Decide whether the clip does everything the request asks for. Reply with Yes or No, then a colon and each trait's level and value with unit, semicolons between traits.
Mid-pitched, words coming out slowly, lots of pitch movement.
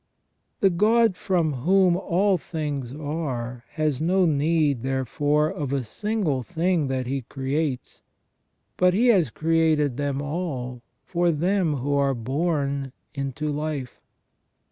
No: medium, 150 Hz; slow, 125 wpm; average, 4.1 semitones